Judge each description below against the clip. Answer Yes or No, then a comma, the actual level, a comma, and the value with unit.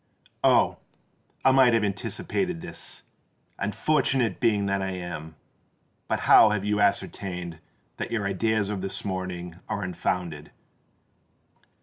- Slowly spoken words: Yes, slow, 115 wpm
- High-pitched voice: No, low, 100 Hz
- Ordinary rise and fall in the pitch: Yes, average, 3.4 semitones